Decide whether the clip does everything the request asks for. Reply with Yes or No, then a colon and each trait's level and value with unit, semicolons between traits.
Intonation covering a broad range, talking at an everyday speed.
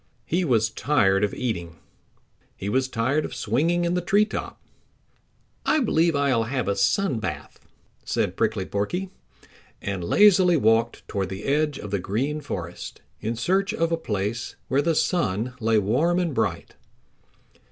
Yes: wide, 8.2 semitones; average, 155 wpm